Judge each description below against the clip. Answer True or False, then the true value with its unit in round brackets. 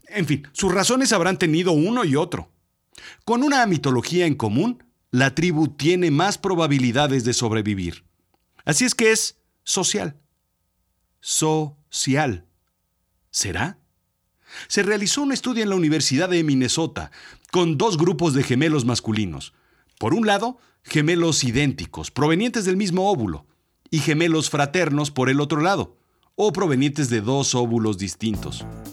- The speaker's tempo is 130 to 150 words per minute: True (135 wpm)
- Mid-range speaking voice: True (150 Hz)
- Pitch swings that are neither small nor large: False (7.1 semitones)